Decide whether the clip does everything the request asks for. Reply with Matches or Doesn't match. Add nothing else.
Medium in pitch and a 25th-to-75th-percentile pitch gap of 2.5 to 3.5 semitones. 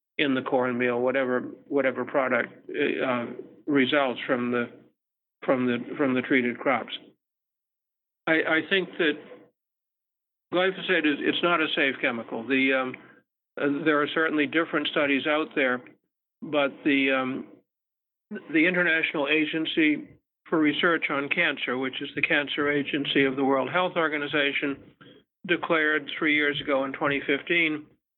Matches